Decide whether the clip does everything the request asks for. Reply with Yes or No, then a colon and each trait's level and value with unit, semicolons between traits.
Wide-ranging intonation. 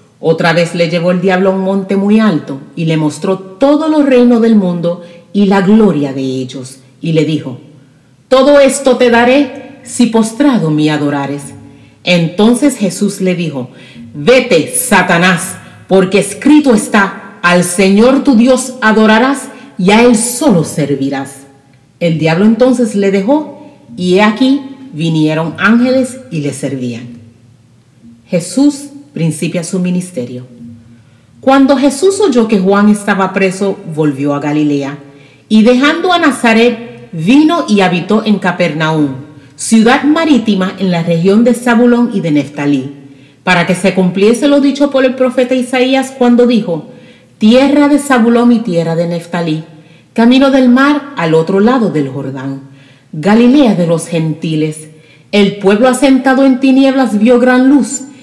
Yes: wide, 8.3 semitones